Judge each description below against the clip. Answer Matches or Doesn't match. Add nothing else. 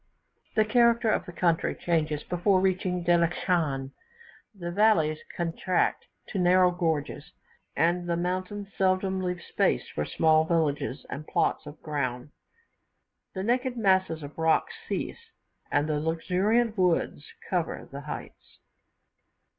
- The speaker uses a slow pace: Matches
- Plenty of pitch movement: Doesn't match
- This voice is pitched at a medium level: Matches